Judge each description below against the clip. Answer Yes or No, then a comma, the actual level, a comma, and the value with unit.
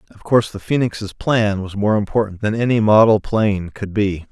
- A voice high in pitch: No, low, 105 Hz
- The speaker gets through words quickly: No, average, 195 wpm